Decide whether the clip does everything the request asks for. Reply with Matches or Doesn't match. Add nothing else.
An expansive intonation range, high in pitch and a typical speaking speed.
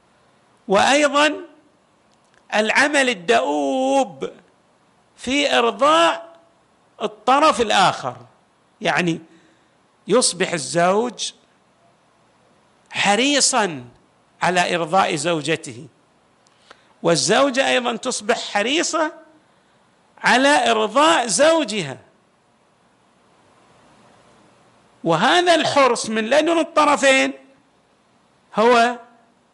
Doesn't match